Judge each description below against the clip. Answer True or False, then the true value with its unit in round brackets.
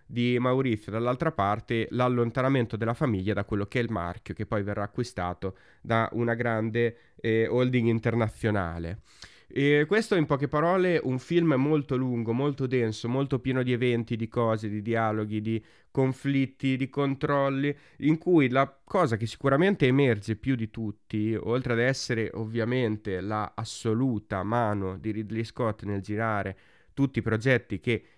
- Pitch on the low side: True (115 Hz)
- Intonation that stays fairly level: False (3.5 semitones)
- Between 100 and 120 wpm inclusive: False (155 wpm)